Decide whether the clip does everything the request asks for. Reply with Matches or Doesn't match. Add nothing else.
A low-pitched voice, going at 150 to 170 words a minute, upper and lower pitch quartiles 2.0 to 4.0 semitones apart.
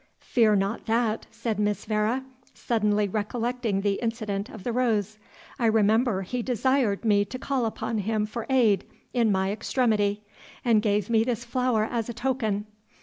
Doesn't match